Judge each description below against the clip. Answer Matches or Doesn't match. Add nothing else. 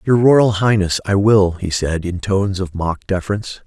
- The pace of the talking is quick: Doesn't match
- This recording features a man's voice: Matches